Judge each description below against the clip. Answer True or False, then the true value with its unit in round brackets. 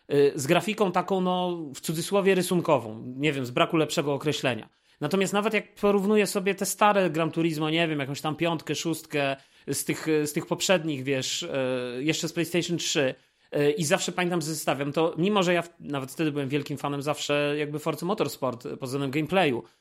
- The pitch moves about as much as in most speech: True (3.7 semitones)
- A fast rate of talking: True (175 wpm)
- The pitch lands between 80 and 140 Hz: False (160 Hz)